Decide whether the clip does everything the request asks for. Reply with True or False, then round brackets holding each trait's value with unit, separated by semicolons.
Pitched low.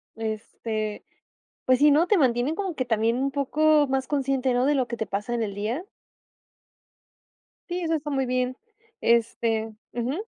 False (255 Hz)